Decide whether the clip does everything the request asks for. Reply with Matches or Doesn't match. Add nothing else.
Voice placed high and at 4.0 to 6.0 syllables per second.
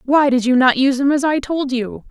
Matches